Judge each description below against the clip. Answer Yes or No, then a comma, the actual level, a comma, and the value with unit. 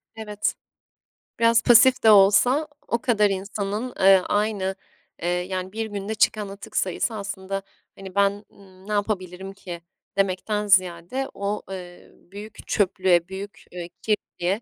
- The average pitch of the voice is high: Yes, high, 200 Hz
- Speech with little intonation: Yes, narrow, 2.1 semitones